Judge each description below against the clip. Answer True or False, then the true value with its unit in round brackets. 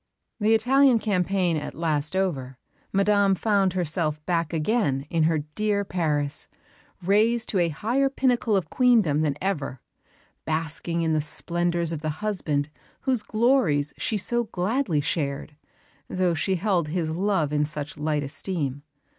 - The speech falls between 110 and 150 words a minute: True (145 wpm)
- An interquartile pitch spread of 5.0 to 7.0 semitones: True (5.5 semitones)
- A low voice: False (175 Hz)